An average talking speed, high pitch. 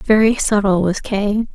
Yes: average, 155 wpm; high, 205 Hz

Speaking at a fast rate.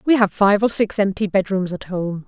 Yes: fast, 265 wpm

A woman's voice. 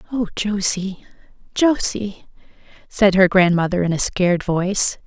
Yes: female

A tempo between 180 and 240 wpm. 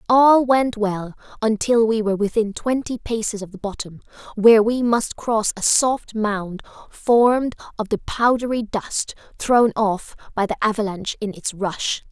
No: average, 160 wpm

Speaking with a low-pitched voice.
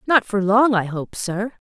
No: high, 210 Hz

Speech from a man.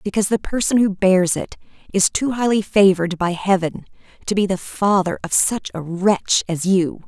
No: female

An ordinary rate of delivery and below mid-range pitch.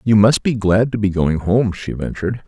No: fast, 240 wpm; low, 105 Hz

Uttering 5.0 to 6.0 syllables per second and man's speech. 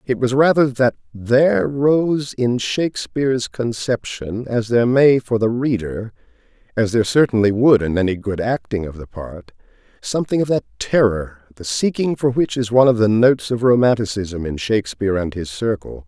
Yes: 5.1 syllables/s; male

